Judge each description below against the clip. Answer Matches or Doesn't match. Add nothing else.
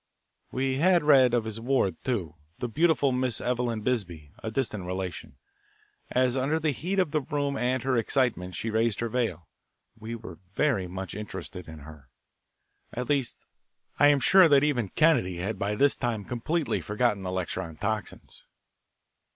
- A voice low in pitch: Matches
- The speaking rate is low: Doesn't match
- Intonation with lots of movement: Matches